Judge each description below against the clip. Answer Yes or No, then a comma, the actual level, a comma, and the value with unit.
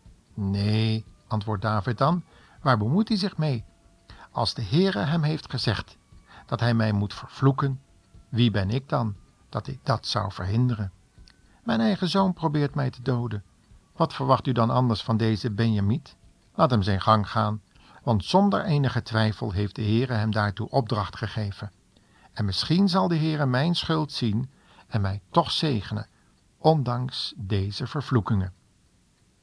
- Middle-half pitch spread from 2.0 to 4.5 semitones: No, average, 4.9 semitones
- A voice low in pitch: Yes, low, 115 Hz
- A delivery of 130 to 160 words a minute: Yes, average, 155 wpm